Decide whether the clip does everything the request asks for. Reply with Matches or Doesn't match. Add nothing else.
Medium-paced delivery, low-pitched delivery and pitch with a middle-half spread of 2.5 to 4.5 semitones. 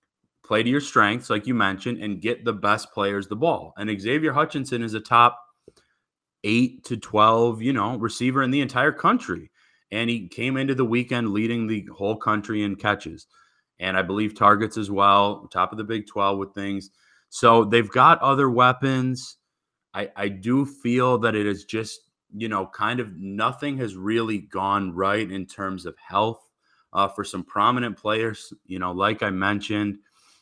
Matches